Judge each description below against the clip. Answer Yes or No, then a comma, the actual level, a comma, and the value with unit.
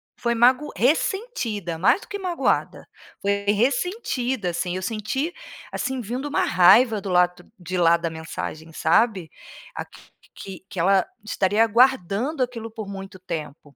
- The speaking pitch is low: No, high, 210 Hz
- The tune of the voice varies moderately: No, wide, 6.0 semitones